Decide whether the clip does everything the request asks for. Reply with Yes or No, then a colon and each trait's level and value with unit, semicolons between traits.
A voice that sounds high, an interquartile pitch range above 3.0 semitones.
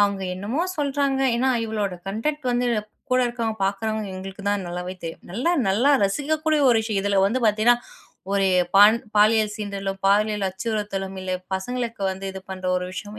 Yes: high, 210 Hz; average, 3.6 semitones